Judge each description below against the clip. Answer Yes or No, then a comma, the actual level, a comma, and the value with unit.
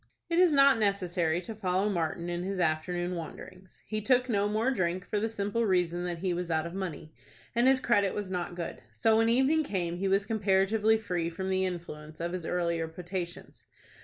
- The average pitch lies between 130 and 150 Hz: No, medium, 185 Hz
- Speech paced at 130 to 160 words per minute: No, average, 200 wpm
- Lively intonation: No, average, 3.8 semitones